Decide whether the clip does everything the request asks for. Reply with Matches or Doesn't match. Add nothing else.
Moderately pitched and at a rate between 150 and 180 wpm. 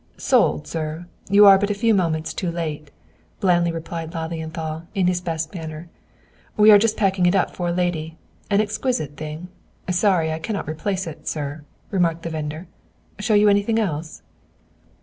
Matches